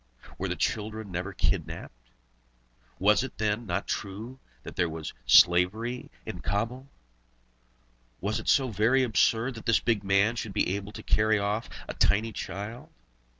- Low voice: Yes, low, 105 Hz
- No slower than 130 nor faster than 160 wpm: Yes, average, 150 wpm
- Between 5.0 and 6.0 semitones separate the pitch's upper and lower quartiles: No, average, 2.8 semitones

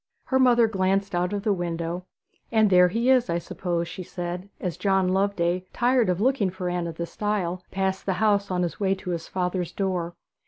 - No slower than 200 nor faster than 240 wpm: Yes, fast, 205 wpm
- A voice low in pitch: No, medium, 185 Hz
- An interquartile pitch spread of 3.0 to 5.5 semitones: No, narrow, 2.4 semitones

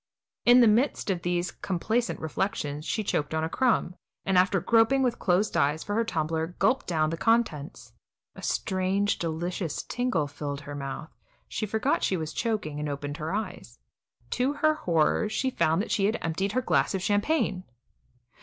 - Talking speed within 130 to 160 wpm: No, average, 175 wpm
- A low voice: No, medium, 185 Hz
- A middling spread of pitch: No, wide, 6.2 semitones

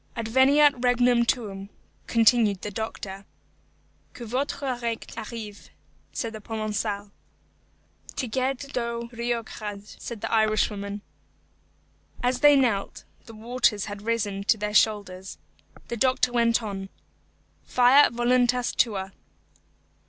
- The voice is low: No, high, 230 Hz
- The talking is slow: Yes, slow, 110 wpm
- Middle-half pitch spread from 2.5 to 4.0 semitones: Yes, average, 2.9 semitones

